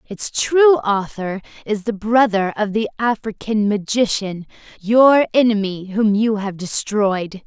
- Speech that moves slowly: Yes, slow, 130 wpm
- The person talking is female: Yes, female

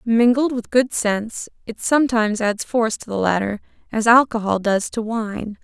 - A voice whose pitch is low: No, high, 225 Hz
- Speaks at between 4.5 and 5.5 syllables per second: Yes, 5.0 syllables/s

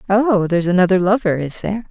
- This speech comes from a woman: Yes, female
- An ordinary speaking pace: Yes, average, 190 wpm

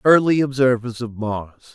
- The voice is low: Yes, low, 125 Hz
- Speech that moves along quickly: No, average, 140 wpm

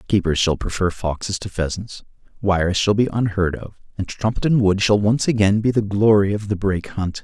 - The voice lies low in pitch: Yes, low, 100 Hz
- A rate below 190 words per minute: No, average, 200 wpm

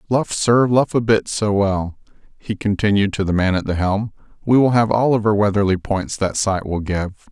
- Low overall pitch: Yes, low, 105 Hz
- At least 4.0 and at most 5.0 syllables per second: Yes, 4.9 syllables/s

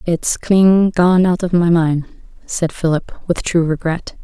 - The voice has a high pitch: No, medium, 170 Hz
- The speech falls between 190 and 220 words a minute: No, average, 170 wpm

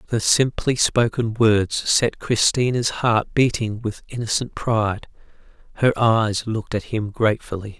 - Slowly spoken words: Yes, slow, 130 wpm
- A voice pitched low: Yes, low, 110 Hz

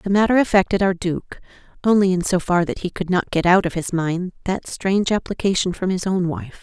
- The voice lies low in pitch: No, medium, 185 Hz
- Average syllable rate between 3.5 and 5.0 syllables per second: No, 5.5 syllables/s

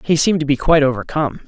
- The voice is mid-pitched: Yes, medium, 145 Hz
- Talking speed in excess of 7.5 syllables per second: Yes, 8.2 syllables/s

